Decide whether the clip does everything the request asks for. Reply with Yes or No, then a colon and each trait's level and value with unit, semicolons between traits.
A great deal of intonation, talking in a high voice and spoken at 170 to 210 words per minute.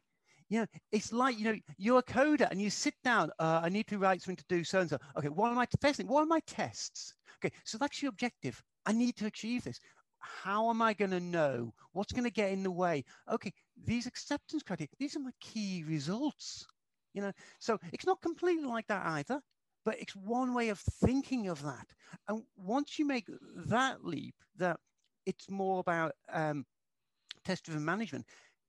Yes: wide, 5.9 semitones; high, 210 Hz; average, 200 wpm